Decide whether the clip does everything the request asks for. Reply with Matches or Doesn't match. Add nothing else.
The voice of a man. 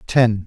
Matches